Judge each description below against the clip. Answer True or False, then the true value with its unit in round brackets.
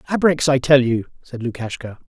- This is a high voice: False (135 Hz)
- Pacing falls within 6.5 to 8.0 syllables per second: False (5.3 syllables/s)